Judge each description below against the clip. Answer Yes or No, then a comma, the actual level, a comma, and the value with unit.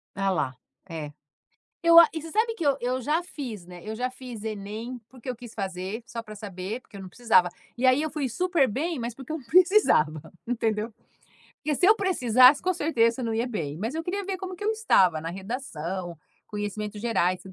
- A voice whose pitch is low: No, high, 235 Hz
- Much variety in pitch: Yes, wide, 7.4 semitones